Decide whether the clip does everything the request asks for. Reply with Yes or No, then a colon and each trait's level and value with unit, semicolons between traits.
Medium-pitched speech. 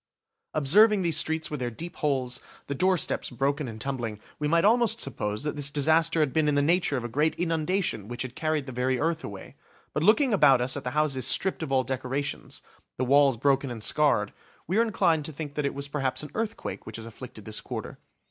Yes: medium, 145 Hz